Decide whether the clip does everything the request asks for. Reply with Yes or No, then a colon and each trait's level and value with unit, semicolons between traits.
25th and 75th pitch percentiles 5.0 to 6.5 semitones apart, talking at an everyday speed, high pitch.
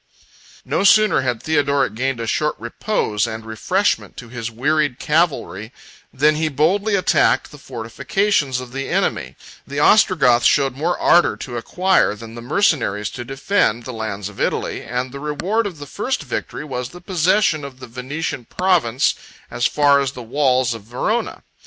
No: wide, 5.4 semitones; average, 165 wpm; low, 135 Hz